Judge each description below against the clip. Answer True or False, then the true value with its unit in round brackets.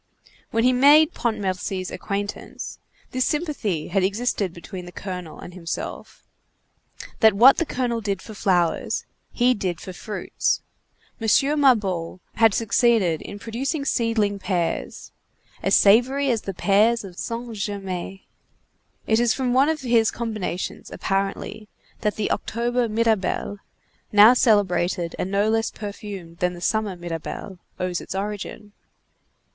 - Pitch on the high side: True (210 Hz)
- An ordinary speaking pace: False (130 wpm)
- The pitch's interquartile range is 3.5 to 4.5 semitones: True (3.9 semitones)